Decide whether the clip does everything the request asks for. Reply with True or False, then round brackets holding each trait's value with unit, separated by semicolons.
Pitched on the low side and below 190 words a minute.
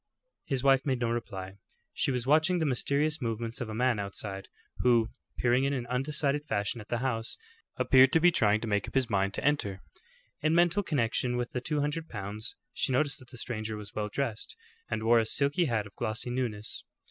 False (120 Hz; 205 wpm)